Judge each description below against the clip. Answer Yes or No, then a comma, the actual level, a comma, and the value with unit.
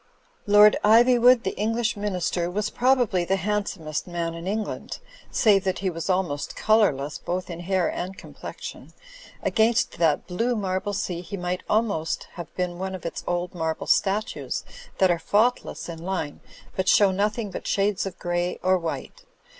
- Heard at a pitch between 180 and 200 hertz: Yes, high, 190 Hz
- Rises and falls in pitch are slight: No, average, 3.2 semitones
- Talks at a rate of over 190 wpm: No, average, 160 wpm